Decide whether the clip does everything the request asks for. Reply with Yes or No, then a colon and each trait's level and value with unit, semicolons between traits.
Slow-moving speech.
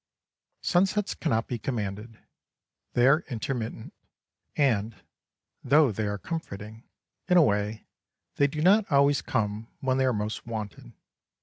Yes: slow, 130 wpm